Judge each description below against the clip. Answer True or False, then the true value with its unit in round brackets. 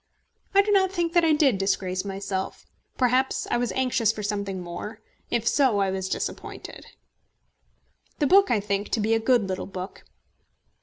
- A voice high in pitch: True (220 Hz)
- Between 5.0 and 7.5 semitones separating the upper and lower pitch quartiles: True (5.3 semitones)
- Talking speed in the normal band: True (170 wpm)